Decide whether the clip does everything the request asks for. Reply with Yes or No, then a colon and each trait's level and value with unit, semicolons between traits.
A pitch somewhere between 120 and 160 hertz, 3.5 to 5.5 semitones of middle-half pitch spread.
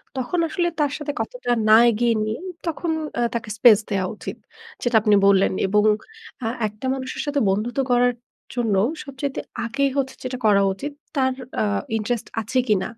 No: high, 240 Hz; average, 4.0 semitones